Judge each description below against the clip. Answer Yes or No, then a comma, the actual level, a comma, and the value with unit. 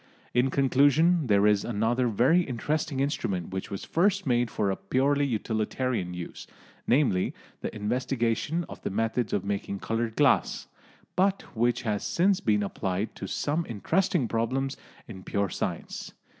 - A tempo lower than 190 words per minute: Yes, average, 145 wpm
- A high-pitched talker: No, low, 120 Hz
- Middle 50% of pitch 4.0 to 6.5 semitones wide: Yes, wide, 5.4 semitones